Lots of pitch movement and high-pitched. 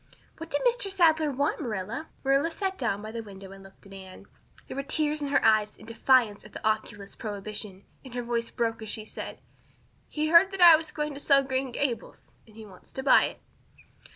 Yes: wide, 5.9 semitones; high, 240 Hz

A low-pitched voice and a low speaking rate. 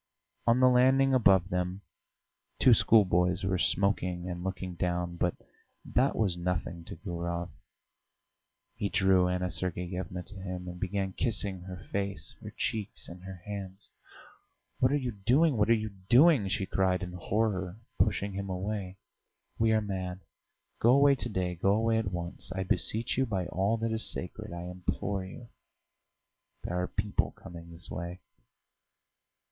No: very low, 95 Hz; average, 155 wpm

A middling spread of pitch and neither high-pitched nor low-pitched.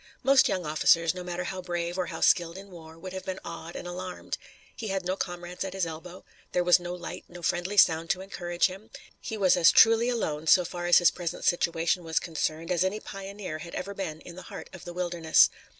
No: narrow, 1.9 semitones; medium, 175 Hz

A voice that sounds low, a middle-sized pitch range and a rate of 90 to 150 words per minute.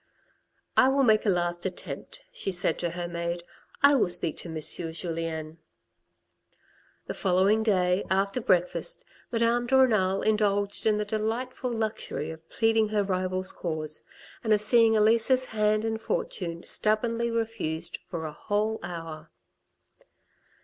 No: high, 205 Hz; average, 4.4 semitones; average, 145 wpm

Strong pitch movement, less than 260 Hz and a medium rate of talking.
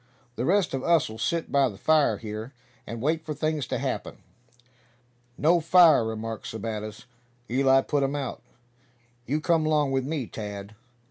Yes: wide, 5.7 semitones; low, 135 Hz; average, 155 wpm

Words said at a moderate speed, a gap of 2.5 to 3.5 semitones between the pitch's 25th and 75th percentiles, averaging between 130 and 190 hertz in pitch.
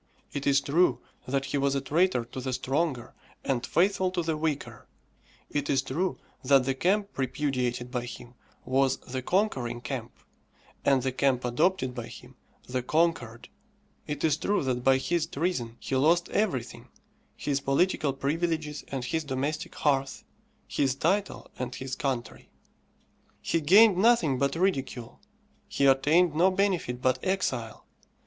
No: average, 150 wpm; average, 4.4 semitones; medium, 140 Hz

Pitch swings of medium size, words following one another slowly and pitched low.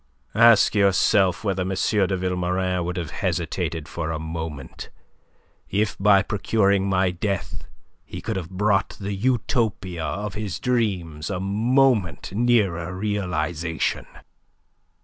Yes: average, 3.1 semitones; slow, 120 wpm; very low, 95 Hz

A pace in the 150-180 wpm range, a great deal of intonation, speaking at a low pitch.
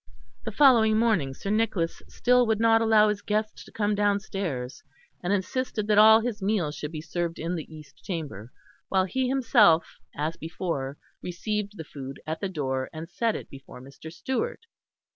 No: average, 175 wpm; wide, 5.7 semitones; high, 195 Hz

